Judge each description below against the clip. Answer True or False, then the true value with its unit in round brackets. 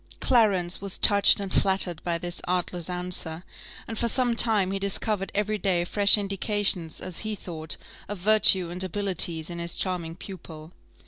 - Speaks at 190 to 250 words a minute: False (160 wpm)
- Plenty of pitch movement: False (2.8 semitones)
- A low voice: False (185 Hz)